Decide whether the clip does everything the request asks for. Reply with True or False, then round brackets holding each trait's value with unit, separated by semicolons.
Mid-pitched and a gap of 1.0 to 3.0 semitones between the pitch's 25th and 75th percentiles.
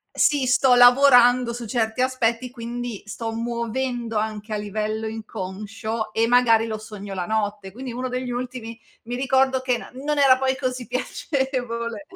False (235 Hz; 2.6 semitones)